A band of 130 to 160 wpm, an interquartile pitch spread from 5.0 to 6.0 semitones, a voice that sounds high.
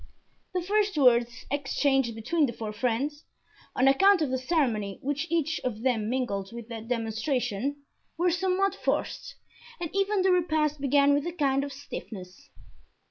Yes: average, 155 wpm; wide, 5.5 semitones; very high, 275 Hz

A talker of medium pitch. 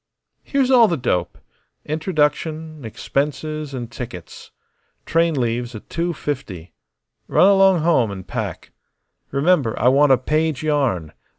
Yes: medium, 145 Hz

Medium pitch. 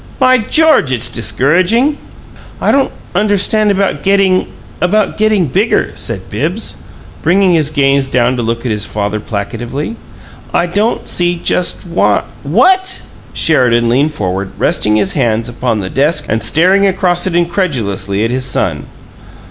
Yes: medium, 150 Hz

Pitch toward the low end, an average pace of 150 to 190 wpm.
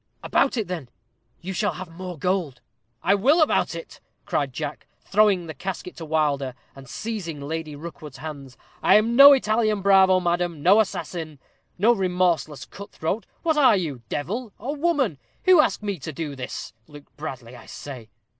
No: medium, 175 Hz; average, 175 wpm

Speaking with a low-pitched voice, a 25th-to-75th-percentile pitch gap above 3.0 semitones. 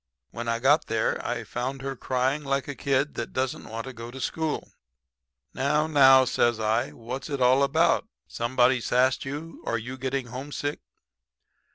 No: low, 130 Hz; narrow, 2.4 semitones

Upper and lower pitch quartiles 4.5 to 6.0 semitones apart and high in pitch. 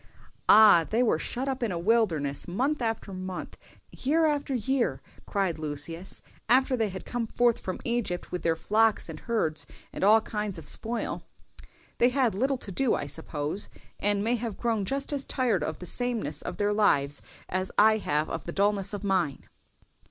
Yes: wide, 5.5 semitones; high, 210 Hz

